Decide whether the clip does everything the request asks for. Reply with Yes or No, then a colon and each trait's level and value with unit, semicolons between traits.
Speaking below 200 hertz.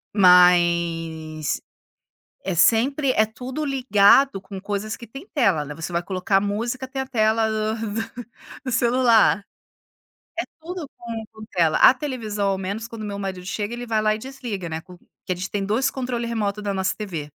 No: high, 215 Hz